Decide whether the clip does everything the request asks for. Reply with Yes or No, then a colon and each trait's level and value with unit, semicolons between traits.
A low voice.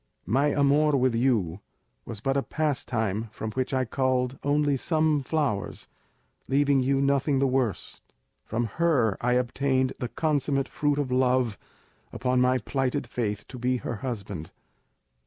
Yes: low, 130 Hz